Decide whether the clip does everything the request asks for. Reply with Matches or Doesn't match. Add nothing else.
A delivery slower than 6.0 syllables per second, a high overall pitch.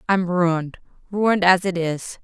Doesn't match